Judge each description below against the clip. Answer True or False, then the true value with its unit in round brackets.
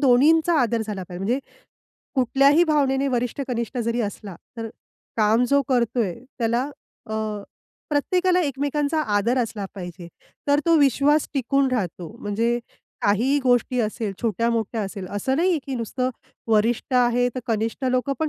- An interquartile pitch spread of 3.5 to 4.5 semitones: True (3.9 semitones)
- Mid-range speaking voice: False (245 Hz)